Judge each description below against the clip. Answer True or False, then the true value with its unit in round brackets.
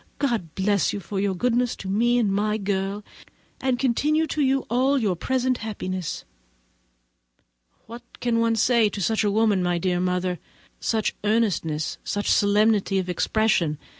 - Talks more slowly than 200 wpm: True (155 wpm)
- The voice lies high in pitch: True (210 Hz)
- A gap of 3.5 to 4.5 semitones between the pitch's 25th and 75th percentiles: True (3.8 semitones)